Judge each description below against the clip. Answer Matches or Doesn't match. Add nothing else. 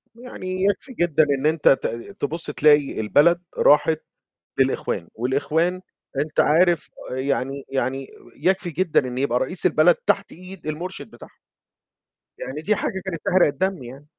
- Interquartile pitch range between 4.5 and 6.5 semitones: Matches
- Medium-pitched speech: Matches